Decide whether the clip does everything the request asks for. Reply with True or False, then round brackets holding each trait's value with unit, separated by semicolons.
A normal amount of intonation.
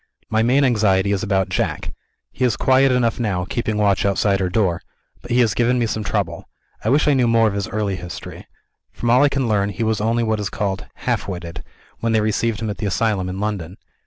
True (3.2 semitones)